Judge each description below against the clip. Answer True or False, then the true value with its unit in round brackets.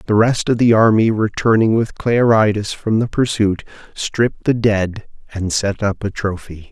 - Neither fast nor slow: True (170 wpm)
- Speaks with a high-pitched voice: False (105 Hz)